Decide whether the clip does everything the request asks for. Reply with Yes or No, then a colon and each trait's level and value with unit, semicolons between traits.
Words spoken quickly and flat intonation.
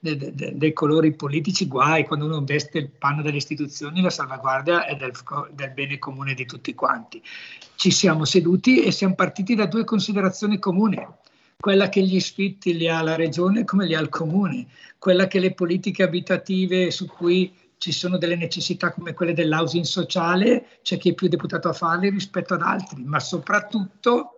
No: fast, 180 wpm; average, 3.4 semitones